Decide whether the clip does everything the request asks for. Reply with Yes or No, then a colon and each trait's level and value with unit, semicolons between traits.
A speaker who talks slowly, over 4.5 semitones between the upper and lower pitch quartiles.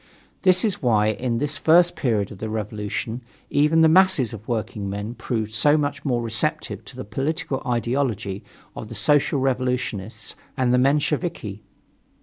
No: average, 150 wpm; average, 5.1 semitones